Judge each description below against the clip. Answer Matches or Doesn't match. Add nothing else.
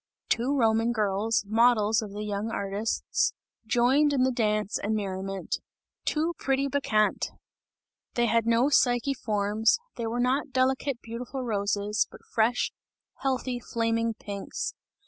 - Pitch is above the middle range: Matches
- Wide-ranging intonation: Doesn't match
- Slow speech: Matches